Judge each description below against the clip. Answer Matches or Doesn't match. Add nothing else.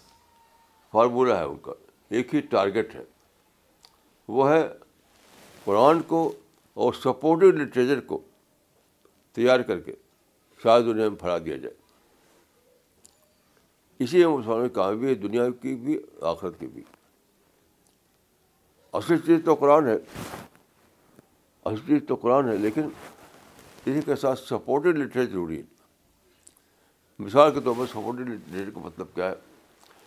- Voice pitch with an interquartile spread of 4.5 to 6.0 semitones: Matches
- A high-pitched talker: Doesn't match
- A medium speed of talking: Matches